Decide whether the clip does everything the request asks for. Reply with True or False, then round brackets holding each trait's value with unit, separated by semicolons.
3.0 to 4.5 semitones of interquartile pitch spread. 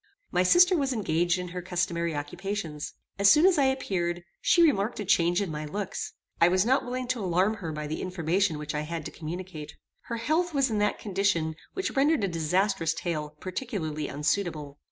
False (5.2 semitones)